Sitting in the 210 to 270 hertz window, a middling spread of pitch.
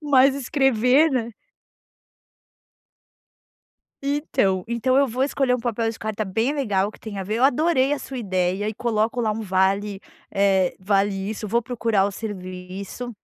Yes: high, 225 Hz; average, 4.6 semitones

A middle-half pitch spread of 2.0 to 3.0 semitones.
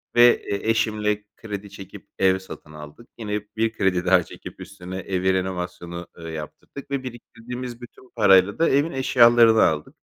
No: average, 4.3 semitones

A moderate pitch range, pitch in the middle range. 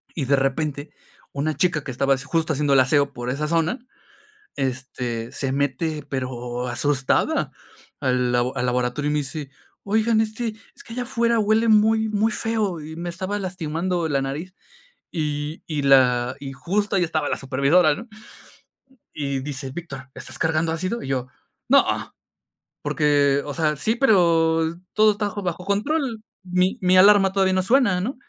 No: wide, 6.1 semitones; medium, 160 Hz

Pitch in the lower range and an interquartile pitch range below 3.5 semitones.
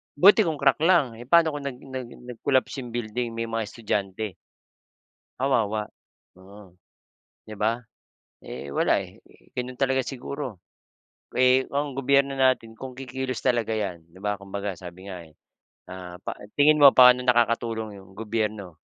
No: low, 120 Hz; average, 4.4 semitones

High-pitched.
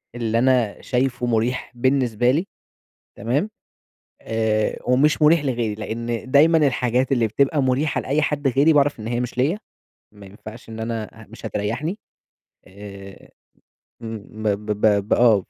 No: low, 120 Hz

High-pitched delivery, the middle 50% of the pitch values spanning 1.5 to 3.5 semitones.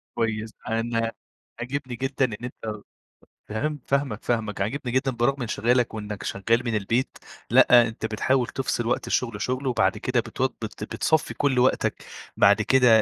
No: low, 120 Hz; average, 2.8 semitones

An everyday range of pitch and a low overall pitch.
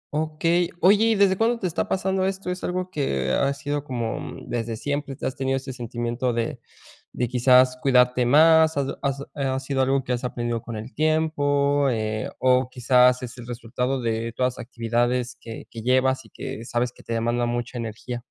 Yes: average, 3.2 semitones; low, 130 Hz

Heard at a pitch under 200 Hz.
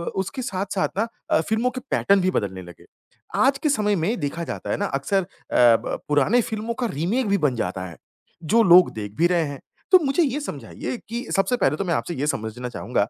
Yes: medium, 185 Hz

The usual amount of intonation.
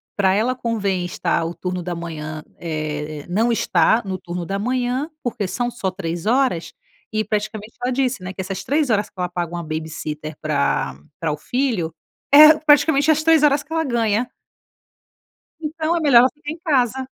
No: wide, 7.3 semitones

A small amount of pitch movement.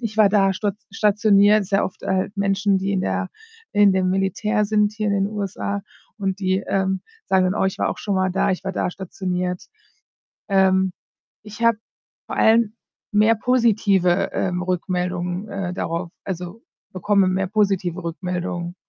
Yes: narrow, 2.0 semitones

